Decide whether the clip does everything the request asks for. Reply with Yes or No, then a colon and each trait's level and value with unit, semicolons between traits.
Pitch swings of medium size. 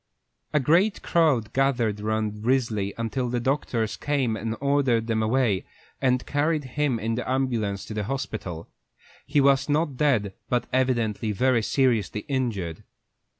Yes: average, 3.8 semitones